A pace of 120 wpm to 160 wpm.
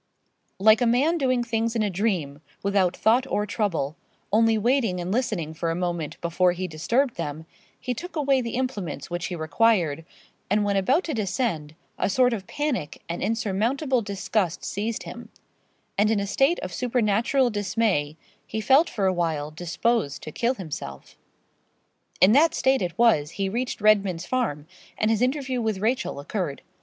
No: average, 170 wpm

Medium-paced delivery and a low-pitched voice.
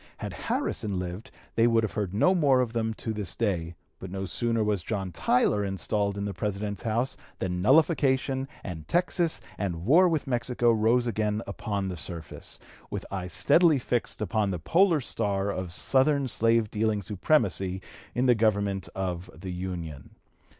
Yes: average, 165 wpm; low, 105 Hz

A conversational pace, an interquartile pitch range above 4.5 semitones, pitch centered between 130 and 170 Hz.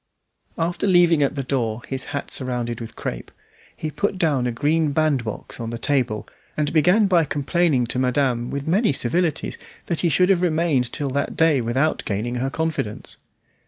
Yes: average, 175 wpm; average, 4.9 semitones; medium, 140 Hz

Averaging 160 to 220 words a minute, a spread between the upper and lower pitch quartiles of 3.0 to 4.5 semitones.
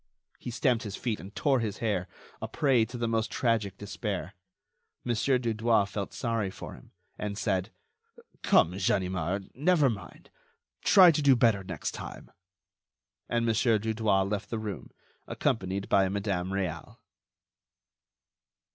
No: slow, 135 wpm; average, 3.3 semitones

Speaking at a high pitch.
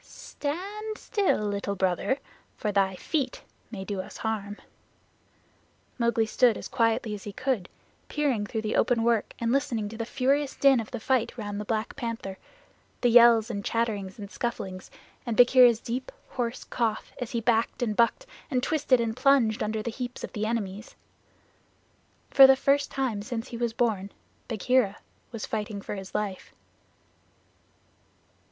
Yes: high, 230 Hz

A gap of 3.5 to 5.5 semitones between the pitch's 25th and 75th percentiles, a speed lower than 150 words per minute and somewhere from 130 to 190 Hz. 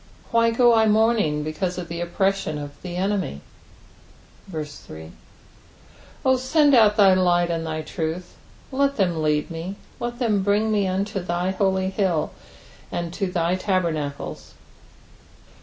Yes: average, 4.2 semitones; average, 140 wpm; medium, 185 Hz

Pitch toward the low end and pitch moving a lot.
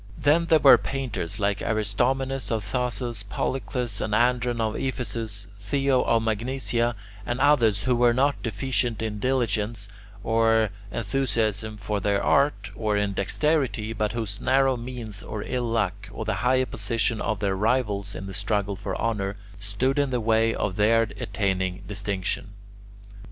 No: low, 110 Hz; average, 3.5 semitones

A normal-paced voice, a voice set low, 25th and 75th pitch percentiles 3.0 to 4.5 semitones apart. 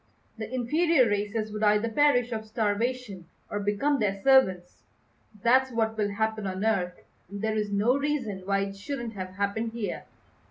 No: average, 165 wpm; high, 220 Hz; average, 3.3 semitones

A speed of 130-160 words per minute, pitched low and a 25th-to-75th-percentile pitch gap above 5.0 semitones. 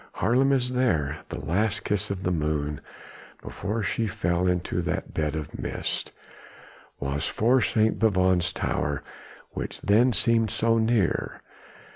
Yes: slow, 135 wpm; low, 100 Hz; wide, 5.5 semitones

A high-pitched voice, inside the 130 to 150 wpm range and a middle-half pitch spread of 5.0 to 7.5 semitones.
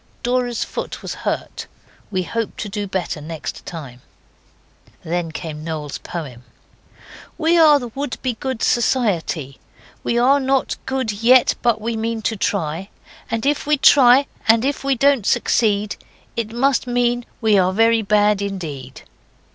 Yes: high, 225 Hz; average, 145 wpm; wide, 5.4 semitones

